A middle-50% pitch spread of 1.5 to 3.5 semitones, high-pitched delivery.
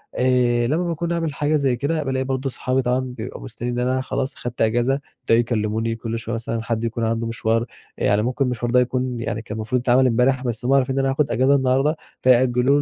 No: narrow, 2.4 semitones; low, 125 Hz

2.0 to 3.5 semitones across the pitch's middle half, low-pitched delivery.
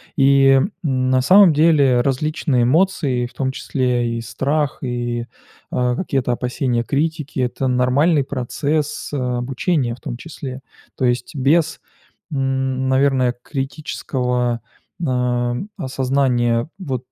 Yes: narrow, 2.5 semitones; low, 130 Hz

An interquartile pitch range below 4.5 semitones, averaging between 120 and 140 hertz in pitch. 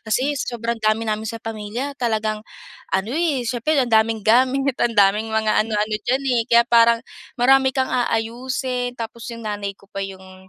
No: narrow, 2.6 semitones; high, 230 Hz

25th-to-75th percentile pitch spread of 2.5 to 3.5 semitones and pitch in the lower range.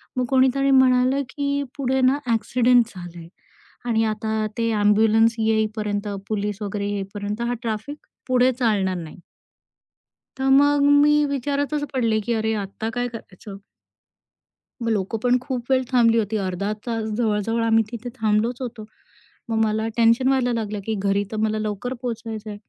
No: average, 3.1 semitones; high, 225 Hz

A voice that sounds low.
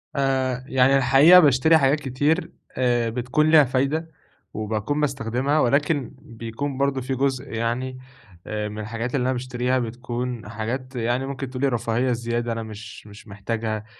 Yes: low, 125 Hz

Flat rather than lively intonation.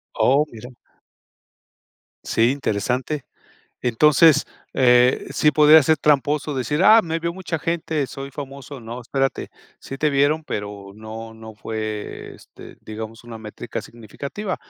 No: average, 5.1 semitones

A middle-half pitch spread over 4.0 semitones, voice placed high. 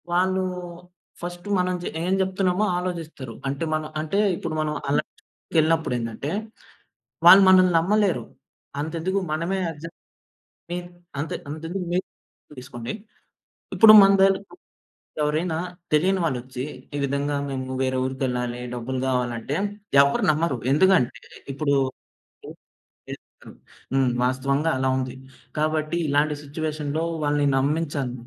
No: average, 4.8 semitones; medium, 155 Hz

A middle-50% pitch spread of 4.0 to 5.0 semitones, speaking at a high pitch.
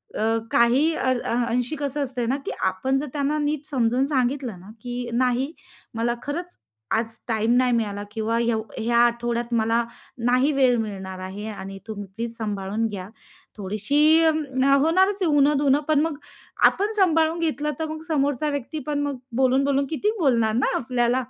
Yes: average, 4.3 semitones; very high, 255 Hz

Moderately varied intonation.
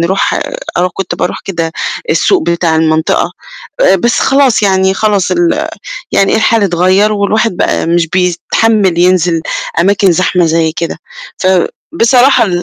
Yes: average, 3.9 semitones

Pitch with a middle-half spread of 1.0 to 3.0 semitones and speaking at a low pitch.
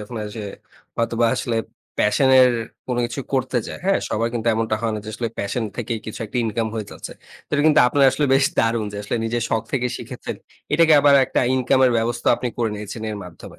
Yes: narrow, 2.6 semitones; low, 115 Hz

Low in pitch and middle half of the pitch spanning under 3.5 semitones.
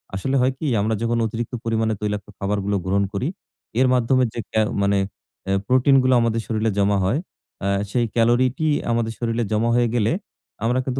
Yes: low, 115 Hz; average, 2.7 semitones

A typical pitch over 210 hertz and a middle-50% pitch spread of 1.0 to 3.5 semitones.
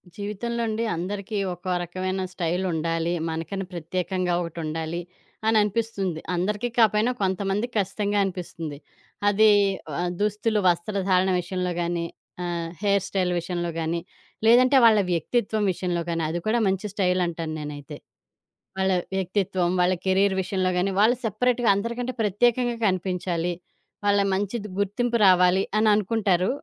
No: high, 190 Hz; average, 3.2 semitones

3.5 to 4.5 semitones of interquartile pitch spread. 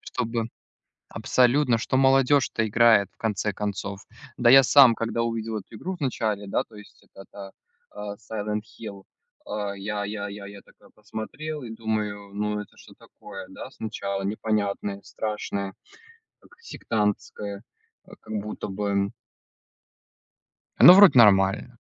No: narrow, 2.5 semitones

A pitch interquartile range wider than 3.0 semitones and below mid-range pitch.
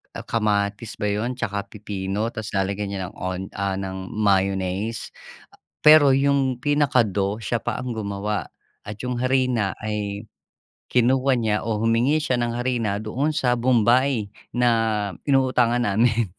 Yes: average, 3.7 semitones; low, 110 Hz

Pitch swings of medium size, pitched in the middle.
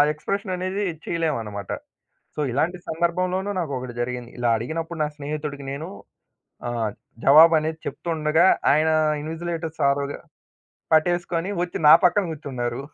Yes: average, 3.6 semitones; medium, 155 Hz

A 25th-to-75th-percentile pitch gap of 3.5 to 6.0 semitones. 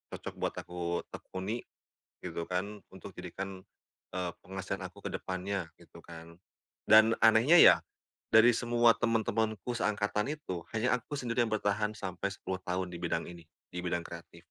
Yes: average, 3.8 semitones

